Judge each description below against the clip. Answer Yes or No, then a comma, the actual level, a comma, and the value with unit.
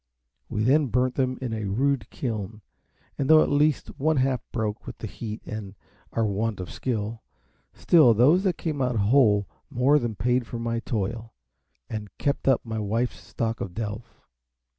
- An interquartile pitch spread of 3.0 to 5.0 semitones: Yes, average, 3.6 semitones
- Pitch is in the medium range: No, low, 115 Hz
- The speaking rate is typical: Yes, average, 180 wpm